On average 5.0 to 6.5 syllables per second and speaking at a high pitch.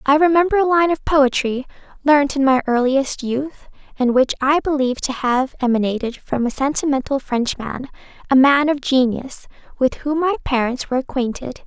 Yes: 5.1 syllables/s; very high, 270 Hz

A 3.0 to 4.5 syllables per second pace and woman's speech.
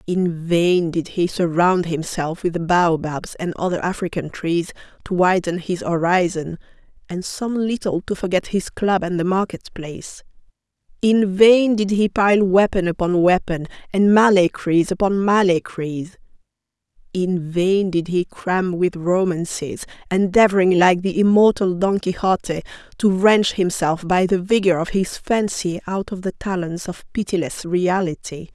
Yes: 4.4 syllables/s; female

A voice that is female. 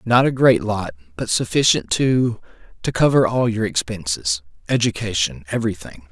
No: male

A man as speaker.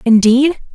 No: female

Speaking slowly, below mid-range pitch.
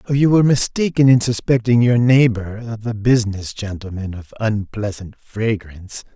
Yes: slow, 125 wpm; low, 110 Hz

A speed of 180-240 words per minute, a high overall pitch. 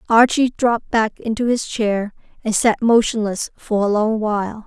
No: average, 165 wpm; high, 220 Hz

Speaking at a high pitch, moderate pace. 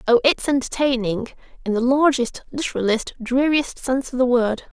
Yes: very high, 260 Hz; average, 150 wpm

